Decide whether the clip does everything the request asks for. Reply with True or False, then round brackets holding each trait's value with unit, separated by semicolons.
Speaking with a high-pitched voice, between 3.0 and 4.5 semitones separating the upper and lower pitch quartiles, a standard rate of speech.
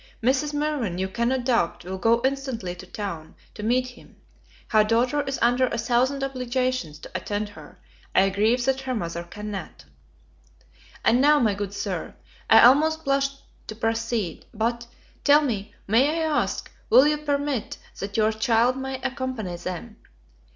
True (240 Hz; 4.2 semitones; 160 wpm)